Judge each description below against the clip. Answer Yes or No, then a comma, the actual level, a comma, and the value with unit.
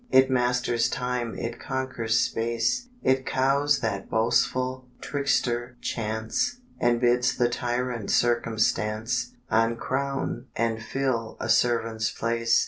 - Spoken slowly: Yes, slow, 110 wpm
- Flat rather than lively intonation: Yes, narrow, 2.2 semitones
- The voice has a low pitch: Yes, low, 120 Hz